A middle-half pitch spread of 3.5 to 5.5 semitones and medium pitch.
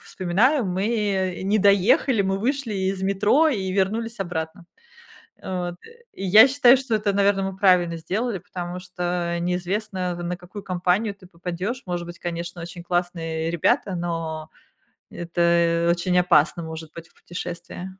No: average, 2.8 semitones; medium, 180 Hz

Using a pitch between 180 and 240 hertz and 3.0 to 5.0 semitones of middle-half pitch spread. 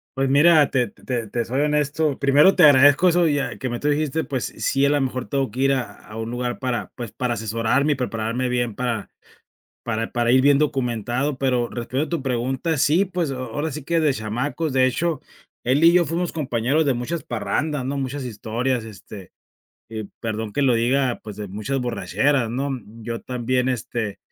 No: low, 130 Hz; average, 3.4 semitones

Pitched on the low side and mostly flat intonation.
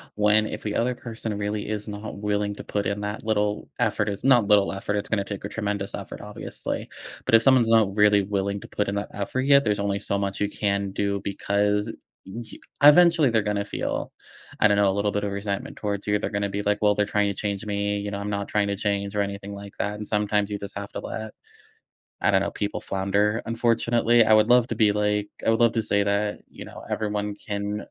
Yes: low, 105 Hz; narrow, 1.1 semitones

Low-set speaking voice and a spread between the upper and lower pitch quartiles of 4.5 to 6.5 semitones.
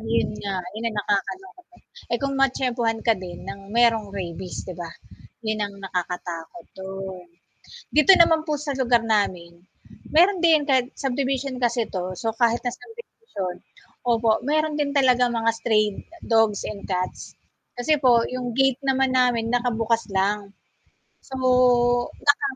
No: high, 235 Hz; average, 4.9 semitones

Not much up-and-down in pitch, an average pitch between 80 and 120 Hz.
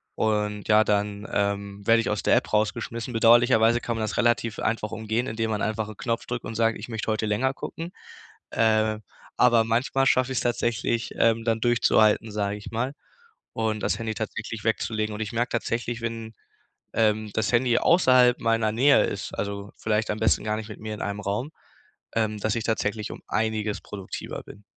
Yes: narrow, 1.7 semitones; low, 110 Hz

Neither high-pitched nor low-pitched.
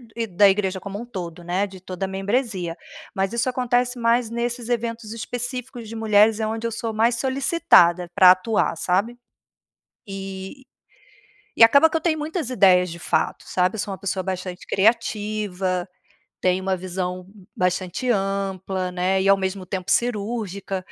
No: high, 200 Hz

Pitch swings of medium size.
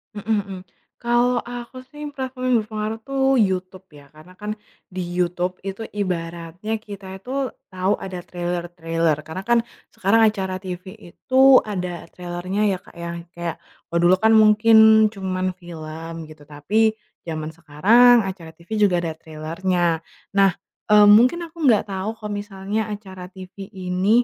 Yes: average, 3.6 semitones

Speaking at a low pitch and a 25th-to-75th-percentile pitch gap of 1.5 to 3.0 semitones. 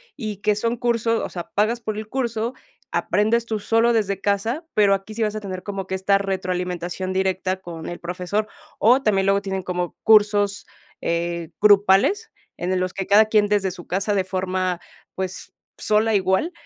No: high, 200 Hz; narrow, 2.6 semitones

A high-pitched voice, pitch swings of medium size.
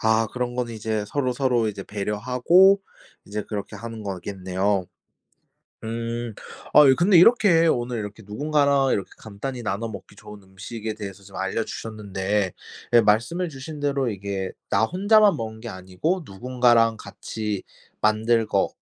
No: low, 115 Hz; average, 4.0 semitones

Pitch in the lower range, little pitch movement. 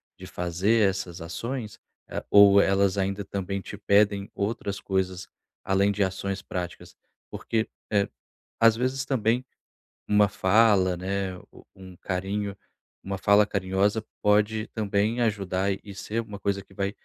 Yes: low, 100 Hz; narrow, 1.6 semitones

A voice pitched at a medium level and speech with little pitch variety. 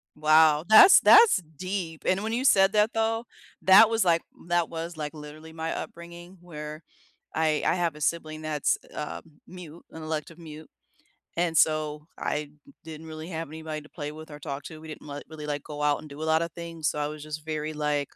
Yes: medium, 160 Hz; narrow, 2.1 semitones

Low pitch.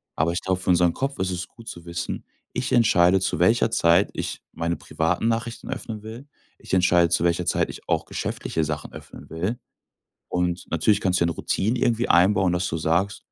Yes: very low, 90 Hz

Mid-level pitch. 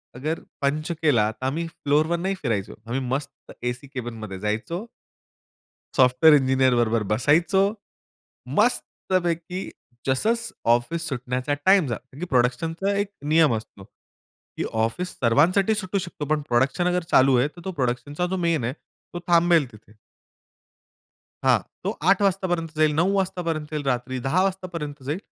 Yes: medium, 150 Hz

